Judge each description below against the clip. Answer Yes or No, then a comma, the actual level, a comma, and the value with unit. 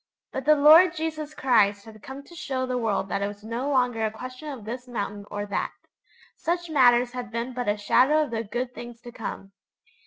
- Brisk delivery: Yes, fast, 215 wpm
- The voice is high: Yes, high, 245 Hz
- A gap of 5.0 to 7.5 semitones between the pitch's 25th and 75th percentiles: No, average, 4.2 semitones